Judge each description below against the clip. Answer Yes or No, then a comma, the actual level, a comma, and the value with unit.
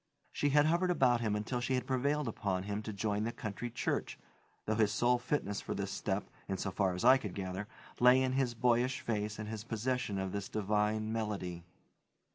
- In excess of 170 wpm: Yes, average, 195 wpm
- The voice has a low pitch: Yes, low, 110 Hz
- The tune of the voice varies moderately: Yes, average, 3.5 semitones